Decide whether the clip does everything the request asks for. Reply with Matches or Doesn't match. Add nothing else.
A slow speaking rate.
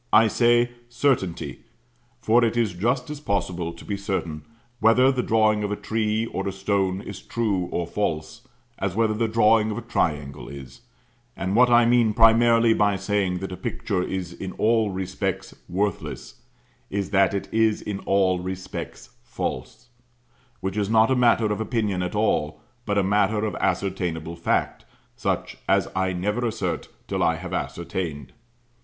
Doesn't match